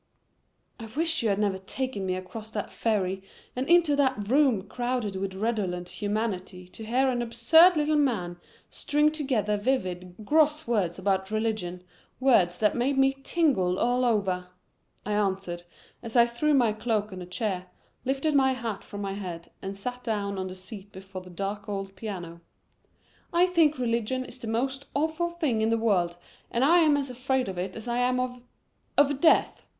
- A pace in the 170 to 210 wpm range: Yes, average, 180 wpm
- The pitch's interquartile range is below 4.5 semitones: No, wide, 5.5 semitones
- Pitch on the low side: No, high, 225 Hz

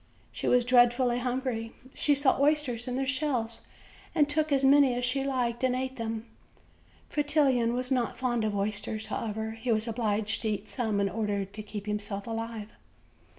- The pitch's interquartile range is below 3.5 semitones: Yes, average, 3.1 semitones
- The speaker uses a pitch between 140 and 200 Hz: No, high, 240 Hz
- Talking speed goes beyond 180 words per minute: No, average, 175 wpm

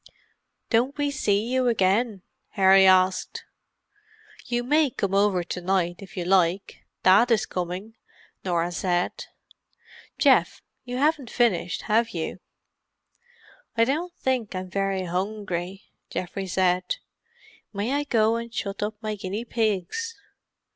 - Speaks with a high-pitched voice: Yes, high, 200 Hz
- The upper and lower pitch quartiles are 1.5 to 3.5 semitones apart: No, average, 4.3 semitones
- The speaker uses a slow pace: Yes, slow, 125 wpm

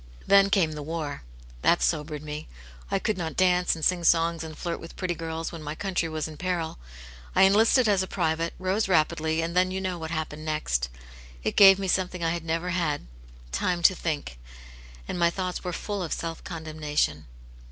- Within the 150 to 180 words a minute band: No, average, 200 wpm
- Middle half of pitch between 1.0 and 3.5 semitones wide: Yes, average, 2.7 semitones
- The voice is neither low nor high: Yes, medium, 165 Hz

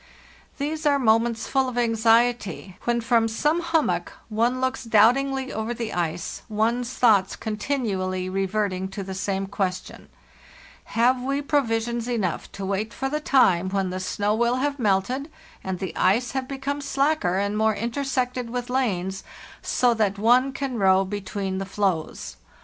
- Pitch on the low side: No, high, 225 Hz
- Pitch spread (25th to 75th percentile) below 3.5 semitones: No, average, 4.8 semitones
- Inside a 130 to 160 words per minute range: Yes, average, 155 wpm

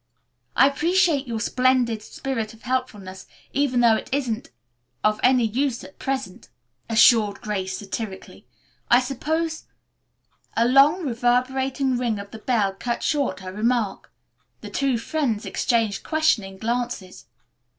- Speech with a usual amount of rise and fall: Yes, average, 3.8 semitones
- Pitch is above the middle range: Yes, high, 240 Hz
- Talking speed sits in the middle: No, slow, 130 wpm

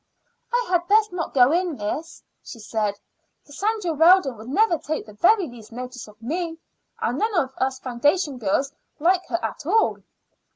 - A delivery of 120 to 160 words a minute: No, average, 170 wpm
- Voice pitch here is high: Yes, very high, 300 Hz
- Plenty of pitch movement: Yes, wide, 6.7 semitones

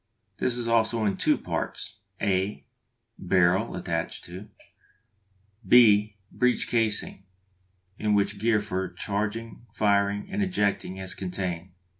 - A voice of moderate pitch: No, low, 105 Hz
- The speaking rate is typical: No, slow, 115 wpm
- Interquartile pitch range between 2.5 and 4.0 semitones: Yes, average, 3.0 semitones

